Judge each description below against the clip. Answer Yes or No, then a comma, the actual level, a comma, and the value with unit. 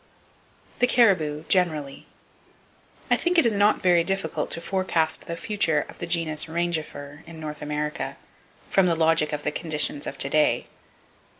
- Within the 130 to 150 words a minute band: No, average, 160 wpm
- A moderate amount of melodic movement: Yes, average, 3.3 semitones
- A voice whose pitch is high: No, medium, 165 Hz